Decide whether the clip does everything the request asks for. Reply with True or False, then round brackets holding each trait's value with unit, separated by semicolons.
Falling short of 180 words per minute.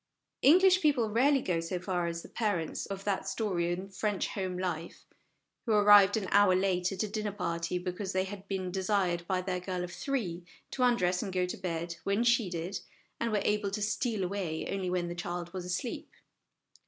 False (200 wpm)